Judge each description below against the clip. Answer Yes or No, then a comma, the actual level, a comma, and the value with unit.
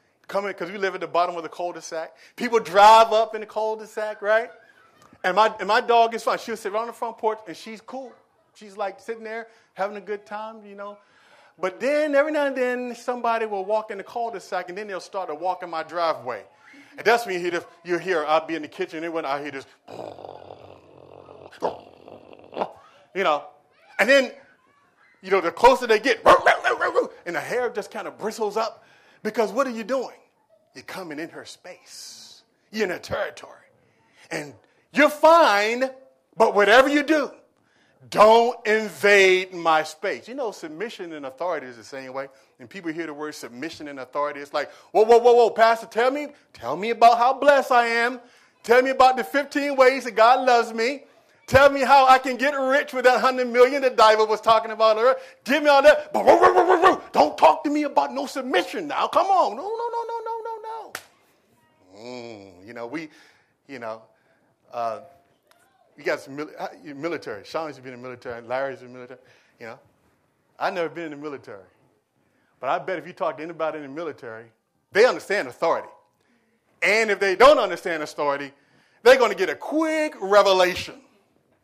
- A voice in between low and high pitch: No, high, 215 Hz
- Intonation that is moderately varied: No, wide, 7.4 semitones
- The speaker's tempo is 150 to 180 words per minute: No, average, 195 wpm